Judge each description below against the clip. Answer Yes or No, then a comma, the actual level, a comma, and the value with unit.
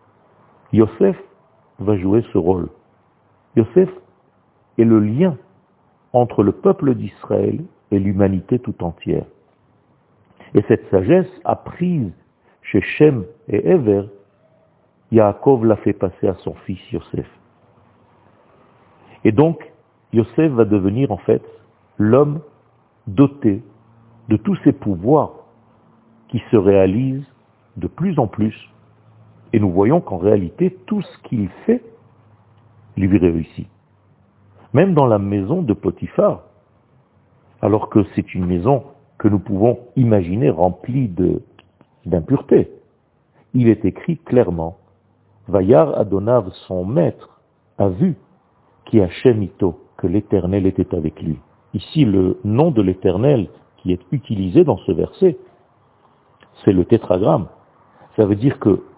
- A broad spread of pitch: No, average, 4.8 semitones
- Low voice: Yes, low, 110 Hz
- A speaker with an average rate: No, slow, 120 wpm